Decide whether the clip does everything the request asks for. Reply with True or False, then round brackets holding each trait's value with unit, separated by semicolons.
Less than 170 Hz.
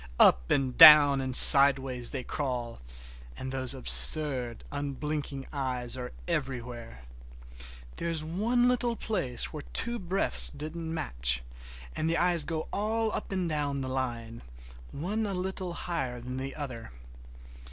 True (140 Hz)